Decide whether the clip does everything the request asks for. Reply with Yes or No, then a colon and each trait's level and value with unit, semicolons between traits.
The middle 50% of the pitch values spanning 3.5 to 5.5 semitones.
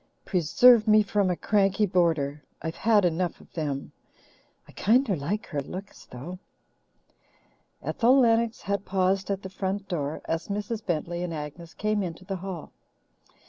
Yes: average, 3.8 semitones